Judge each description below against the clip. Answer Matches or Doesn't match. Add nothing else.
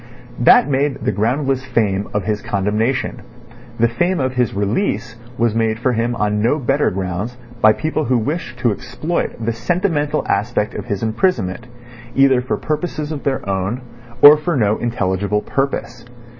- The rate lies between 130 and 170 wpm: Matches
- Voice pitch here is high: Doesn't match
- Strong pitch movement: Doesn't match